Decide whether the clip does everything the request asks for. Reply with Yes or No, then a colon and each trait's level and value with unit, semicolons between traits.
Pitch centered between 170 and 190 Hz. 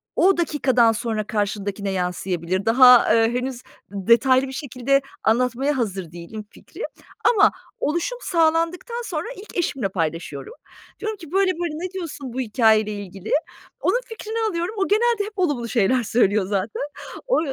No: very high, 250 Hz